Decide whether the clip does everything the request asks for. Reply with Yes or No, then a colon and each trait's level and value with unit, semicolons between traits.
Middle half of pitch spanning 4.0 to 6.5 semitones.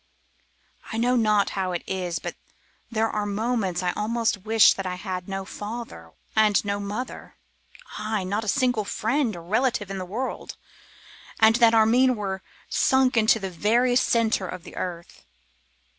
No: average, 3.4 semitones